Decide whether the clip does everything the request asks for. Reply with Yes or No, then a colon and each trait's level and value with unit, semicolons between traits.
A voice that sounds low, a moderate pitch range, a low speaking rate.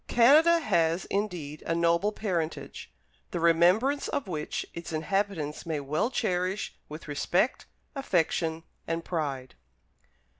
No: medium, 170 Hz; average, 4.4 semitones; slow, 115 wpm